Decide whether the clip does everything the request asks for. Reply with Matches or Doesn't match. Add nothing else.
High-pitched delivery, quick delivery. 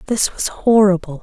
Doesn't match